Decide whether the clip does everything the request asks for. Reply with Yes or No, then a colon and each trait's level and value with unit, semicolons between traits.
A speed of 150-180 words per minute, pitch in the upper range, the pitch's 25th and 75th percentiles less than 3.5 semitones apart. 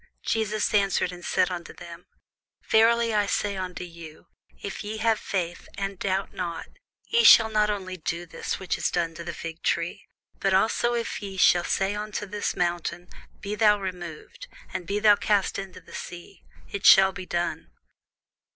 Yes: average, 175 wpm; high, 195 Hz; average, 3.1 semitones